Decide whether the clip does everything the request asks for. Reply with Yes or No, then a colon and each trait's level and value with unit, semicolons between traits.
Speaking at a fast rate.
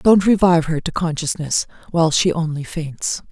No: average, 165 wpm